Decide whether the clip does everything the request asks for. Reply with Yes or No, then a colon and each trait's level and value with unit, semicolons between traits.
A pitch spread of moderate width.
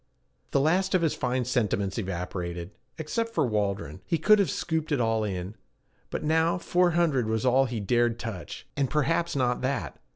No: wide, 7.6 semitones